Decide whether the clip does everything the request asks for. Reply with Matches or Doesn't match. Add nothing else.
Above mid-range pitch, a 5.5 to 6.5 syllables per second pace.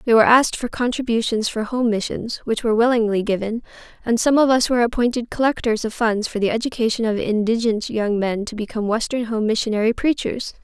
Matches